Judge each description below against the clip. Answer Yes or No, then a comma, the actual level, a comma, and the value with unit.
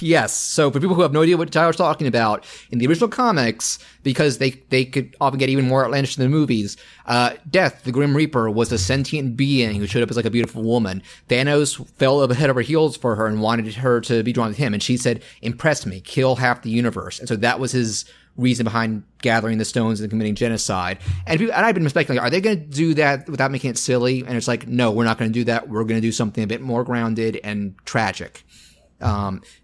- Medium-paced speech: No, fast, 245 wpm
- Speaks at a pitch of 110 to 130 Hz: Yes, low, 125 Hz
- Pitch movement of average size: Yes, average, 3.6 semitones